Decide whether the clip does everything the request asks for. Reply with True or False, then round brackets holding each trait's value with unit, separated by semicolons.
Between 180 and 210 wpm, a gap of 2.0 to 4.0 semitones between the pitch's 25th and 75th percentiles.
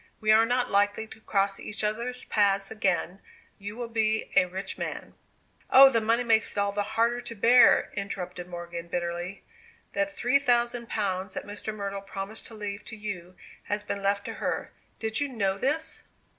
True (185 wpm; 2.9 semitones)